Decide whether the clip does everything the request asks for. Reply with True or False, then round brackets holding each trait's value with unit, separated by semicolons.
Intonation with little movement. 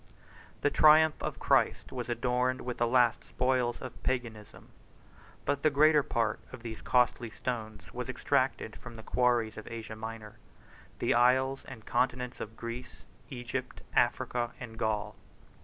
True (2.2 semitones)